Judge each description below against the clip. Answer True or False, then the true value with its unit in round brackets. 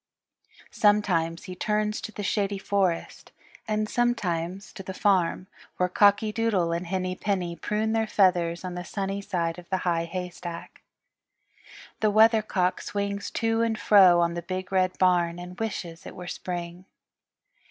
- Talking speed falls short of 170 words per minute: True (150 wpm)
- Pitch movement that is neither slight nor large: True (3.0 semitones)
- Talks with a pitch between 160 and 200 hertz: True (185 Hz)